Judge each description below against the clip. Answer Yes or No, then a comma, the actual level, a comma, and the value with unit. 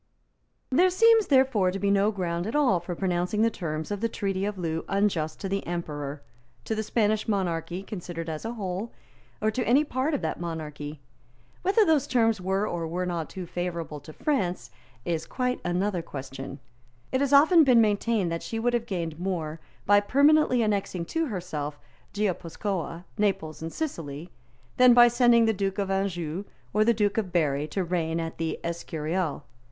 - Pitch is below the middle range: No, high, 190 Hz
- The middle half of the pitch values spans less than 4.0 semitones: No, average, 5.3 semitones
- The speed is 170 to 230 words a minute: Yes, average, 180 wpm